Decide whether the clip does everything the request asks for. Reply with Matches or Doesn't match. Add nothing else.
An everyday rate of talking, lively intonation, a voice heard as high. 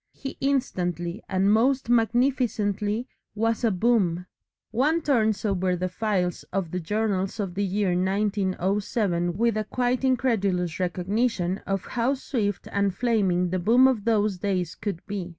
Doesn't match